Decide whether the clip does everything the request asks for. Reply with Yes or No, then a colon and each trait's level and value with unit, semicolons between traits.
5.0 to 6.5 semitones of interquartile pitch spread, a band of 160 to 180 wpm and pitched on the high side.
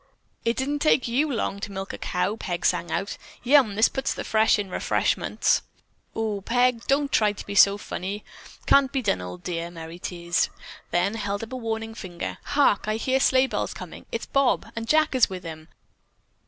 No: wide, 5.6 semitones; average, 195 wpm; high, 215 Hz